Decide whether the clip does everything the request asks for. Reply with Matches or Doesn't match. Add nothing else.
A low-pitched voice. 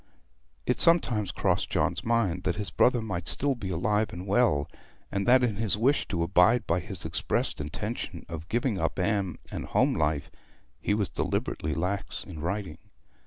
Matches